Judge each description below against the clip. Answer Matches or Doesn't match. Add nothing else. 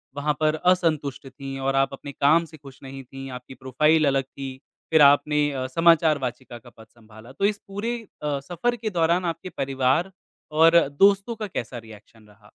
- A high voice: Doesn't match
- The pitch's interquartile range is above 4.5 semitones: Doesn't match